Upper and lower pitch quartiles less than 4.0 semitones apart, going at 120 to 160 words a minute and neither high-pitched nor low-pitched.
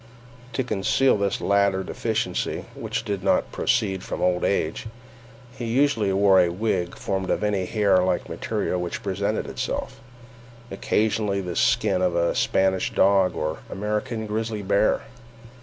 No: average, 2.8 semitones; average, 140 wpm; low, 100 Hz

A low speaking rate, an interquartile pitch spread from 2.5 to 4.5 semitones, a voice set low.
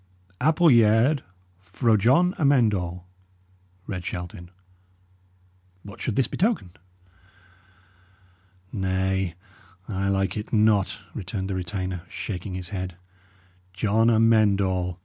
Yes: slow, 100 wpm; average, 3.4 semitones; low, 100 Hz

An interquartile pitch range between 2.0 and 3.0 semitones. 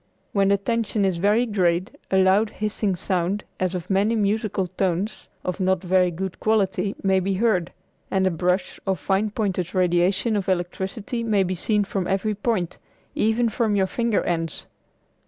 Yes: narrow, 2.5 semitones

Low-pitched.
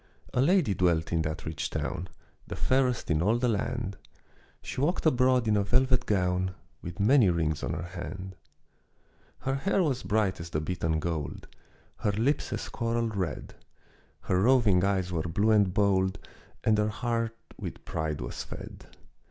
Yes: low, 100 Hz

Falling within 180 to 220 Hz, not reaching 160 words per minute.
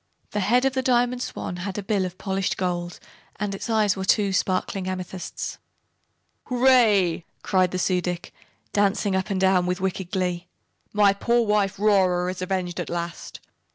No: high, 190 Hz; average, 170 wpm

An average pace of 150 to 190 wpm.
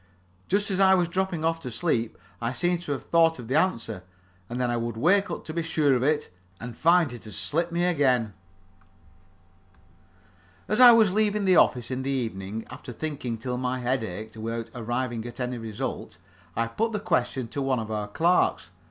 No: average, 200 wpm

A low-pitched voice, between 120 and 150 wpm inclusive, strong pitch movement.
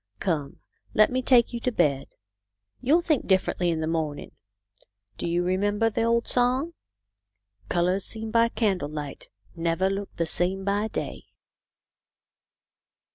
No: high, 190 Hz; average, 145 wpm; wide, 5.9 semitones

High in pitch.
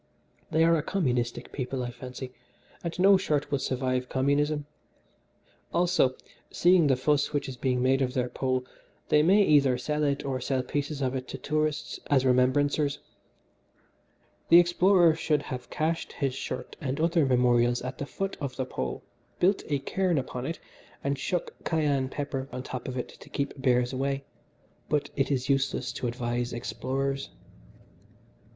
No: low, 135 Hz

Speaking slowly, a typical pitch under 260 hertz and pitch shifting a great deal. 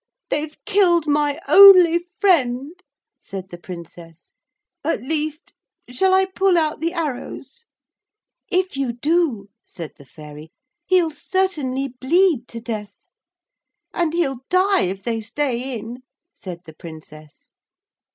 No: slow, 120 wpm; very high, 285 Hz; wide, 8.5 semitones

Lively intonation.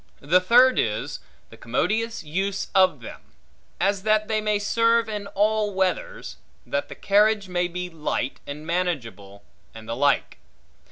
No: average, 4.9 semitones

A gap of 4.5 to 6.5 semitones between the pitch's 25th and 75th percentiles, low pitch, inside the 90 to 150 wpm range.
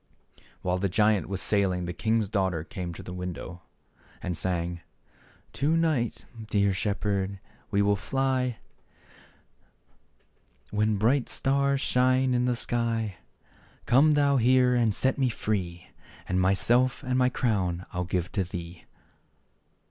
Yes: wide, 5.5 semitones; low, 105 Hz; average, 140 wpm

